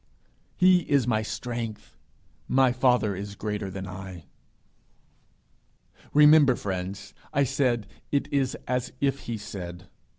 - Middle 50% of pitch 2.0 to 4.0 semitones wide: No, average, 5.2 semitones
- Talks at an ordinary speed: No, slow, 120 wpm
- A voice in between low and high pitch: No, low, 115 Hz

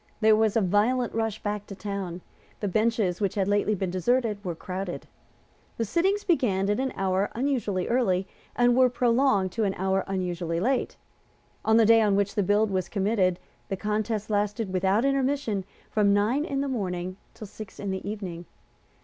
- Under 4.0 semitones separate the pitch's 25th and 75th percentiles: Yes, average, 3.3 semitones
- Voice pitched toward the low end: No, high, 205 Hz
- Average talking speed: Yes, average, 180 wpm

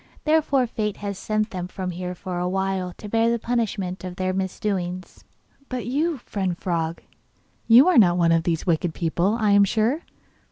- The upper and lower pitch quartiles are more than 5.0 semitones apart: No, average, 4.0 semitones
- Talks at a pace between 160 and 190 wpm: Yes, average, 175 wpm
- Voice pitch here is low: No, high, 190 Hz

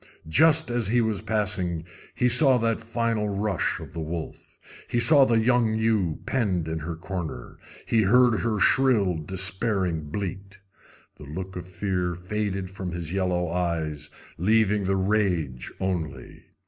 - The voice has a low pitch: Yes, very low, 95 Hz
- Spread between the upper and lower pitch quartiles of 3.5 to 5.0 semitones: Yes, average, 4.3 semitones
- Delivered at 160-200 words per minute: No, average, 150 wpm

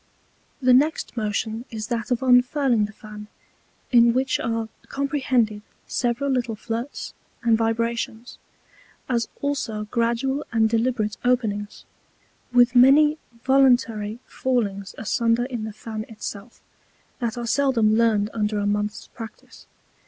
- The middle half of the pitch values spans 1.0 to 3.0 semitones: Yes, narrow, 2.6 semitones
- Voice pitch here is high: Yes, high, 230 Hz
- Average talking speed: No, slow, 125 wpm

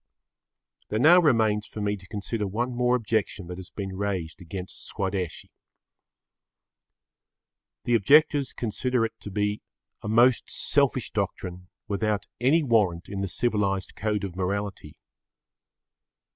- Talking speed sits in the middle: No, slow, 130 wpm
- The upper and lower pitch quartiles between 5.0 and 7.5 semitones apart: No, average, 3.4 semitones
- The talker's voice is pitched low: Yes, low, 105 Hz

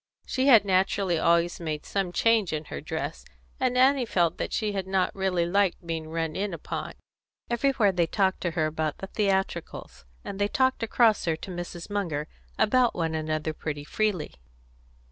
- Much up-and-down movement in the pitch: No, average, 4.2 semitones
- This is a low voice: No, medium, 185 Hz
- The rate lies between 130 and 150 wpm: No, average, 175 wpm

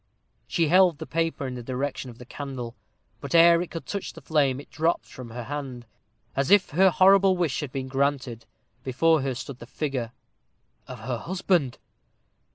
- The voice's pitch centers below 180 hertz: Yes, medium, 140 Hz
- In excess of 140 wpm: Yes, average, 180 wpm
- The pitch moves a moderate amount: Yes, average, 4.5 semitones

